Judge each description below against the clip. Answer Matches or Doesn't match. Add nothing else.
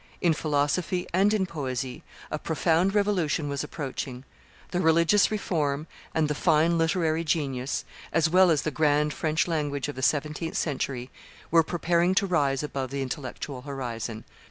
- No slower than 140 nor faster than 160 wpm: Matches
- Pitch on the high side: Doesn't match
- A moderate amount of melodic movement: Matches